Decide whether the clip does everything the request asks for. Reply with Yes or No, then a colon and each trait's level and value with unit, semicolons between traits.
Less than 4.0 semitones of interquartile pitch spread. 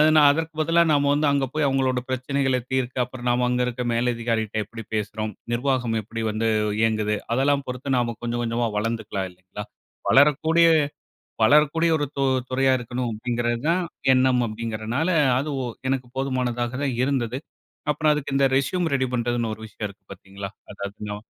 Yes: average, 3.3 semitones